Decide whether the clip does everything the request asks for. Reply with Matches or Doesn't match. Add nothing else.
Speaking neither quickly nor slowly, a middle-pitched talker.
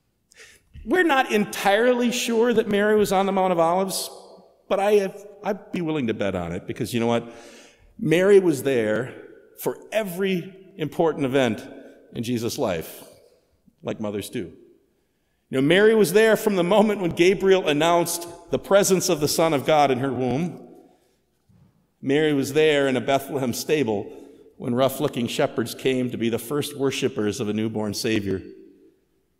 Matches